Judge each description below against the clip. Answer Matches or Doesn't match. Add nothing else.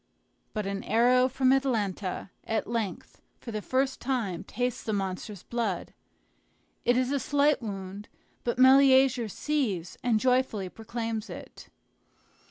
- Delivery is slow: Matches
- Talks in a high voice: Matches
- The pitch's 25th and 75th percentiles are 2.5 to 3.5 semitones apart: Doesn't match